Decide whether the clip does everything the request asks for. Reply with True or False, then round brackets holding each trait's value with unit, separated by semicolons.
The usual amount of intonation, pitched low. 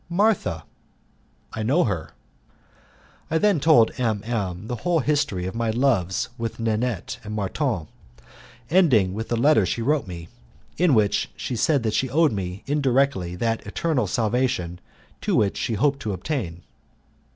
False (6.0 semitones; 115 Hz)